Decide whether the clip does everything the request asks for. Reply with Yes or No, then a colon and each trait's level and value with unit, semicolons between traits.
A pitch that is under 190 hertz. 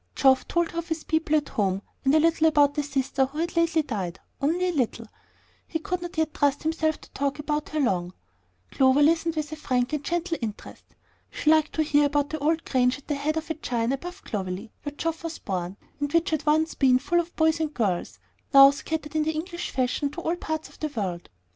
No: very high, 300 Hz